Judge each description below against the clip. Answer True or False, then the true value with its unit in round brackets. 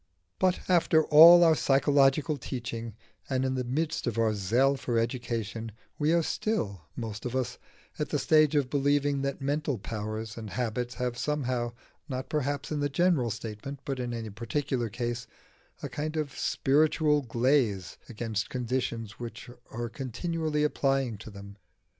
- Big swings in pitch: False (4.1 semitones)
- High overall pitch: False (130 Hz)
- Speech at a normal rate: True (160 wpm)